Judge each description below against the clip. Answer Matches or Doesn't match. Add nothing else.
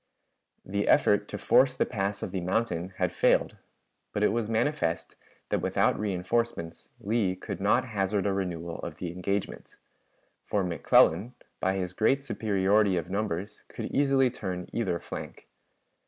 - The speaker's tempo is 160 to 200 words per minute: Doesn't match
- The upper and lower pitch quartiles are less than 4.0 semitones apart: Matches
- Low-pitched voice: Matches